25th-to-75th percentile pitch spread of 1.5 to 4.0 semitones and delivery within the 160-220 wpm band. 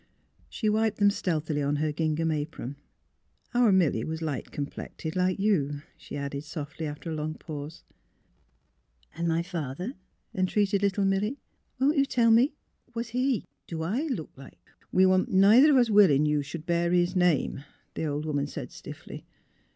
No: wide, 5.5 semitones; average, 180 wpm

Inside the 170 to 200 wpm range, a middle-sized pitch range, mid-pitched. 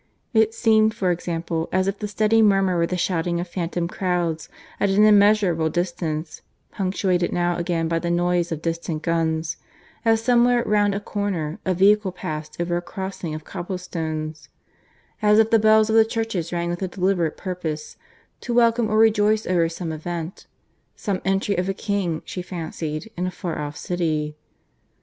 Yes: average, 175 wpm; average, 3.7 semitones; medium, 180 Hz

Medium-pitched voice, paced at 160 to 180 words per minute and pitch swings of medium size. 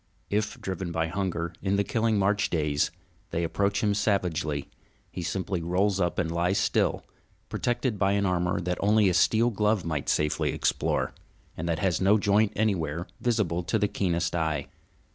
No: very low, 95 Hz; average, 170 wpm; average, 3.5 semitones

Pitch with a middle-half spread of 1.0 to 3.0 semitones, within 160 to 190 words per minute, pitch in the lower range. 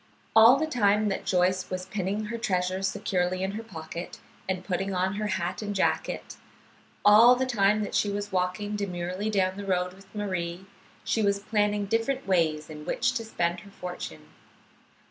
No: narrow, 2.5 semitones; average, 175 wpm; high, 195 Hz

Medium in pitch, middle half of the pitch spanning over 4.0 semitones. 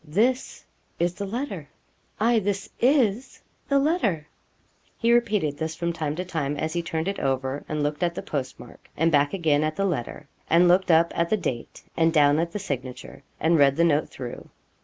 Yes: medium, 165 Hz; average, 5.0 semitones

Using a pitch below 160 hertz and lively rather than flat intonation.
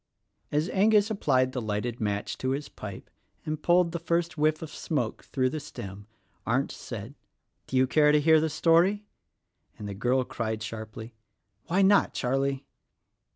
Yes: low, 135 Hz; wide, 6.1 semitones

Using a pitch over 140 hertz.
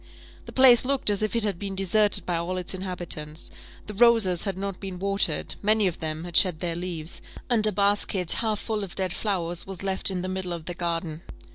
Yes: high, 190 Hz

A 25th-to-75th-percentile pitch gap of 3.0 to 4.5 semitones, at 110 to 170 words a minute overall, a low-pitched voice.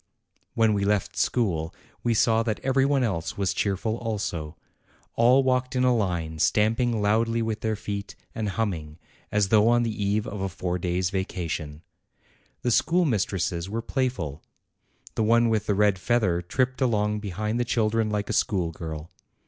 Yes: average, 3.8 semitones; average, 165 wpm; low, 105 Hz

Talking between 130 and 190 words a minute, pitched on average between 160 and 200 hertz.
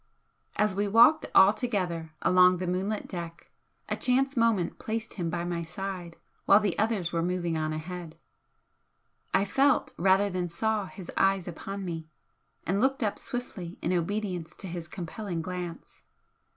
Yes: average, 155 wpm; medium, 185 Hz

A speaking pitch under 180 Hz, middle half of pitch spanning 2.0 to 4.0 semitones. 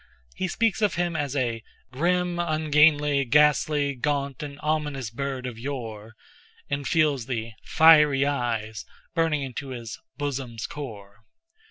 Yes: medium, 140 Hz; average, 3.6 semitones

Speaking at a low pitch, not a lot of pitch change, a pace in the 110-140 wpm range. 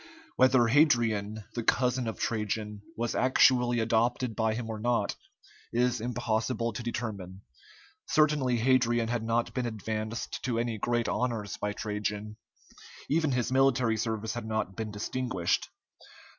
Yes: low, 115 Hz; narrow, 2.2 semitones; slow, 135 wpm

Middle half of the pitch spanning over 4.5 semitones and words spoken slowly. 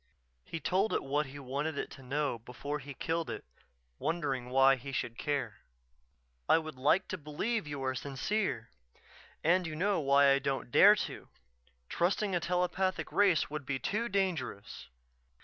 No: average, 5.0 semitones; average, 165 wpm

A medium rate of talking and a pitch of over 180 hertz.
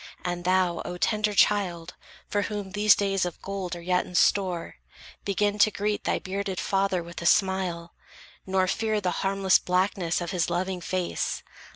Yes: average, 170 wpm; high, 190 Hz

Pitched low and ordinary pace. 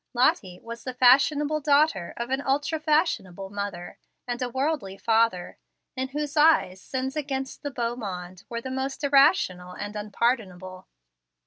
No: high, 245 Hz; average, 145 wpm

